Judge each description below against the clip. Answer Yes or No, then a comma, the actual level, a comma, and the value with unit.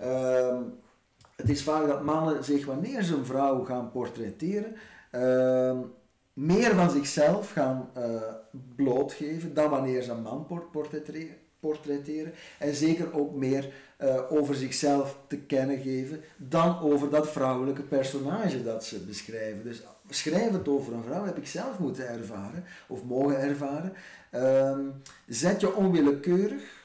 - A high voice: No, medium, 140 Hz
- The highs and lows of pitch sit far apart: No, average, 3.3 semitones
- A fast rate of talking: No, slow, 135 wpm